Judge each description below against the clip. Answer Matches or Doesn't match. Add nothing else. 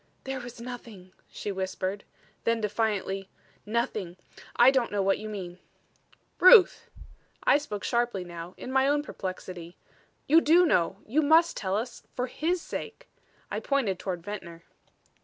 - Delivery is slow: Doesn't match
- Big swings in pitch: Matches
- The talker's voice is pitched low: Doesn't match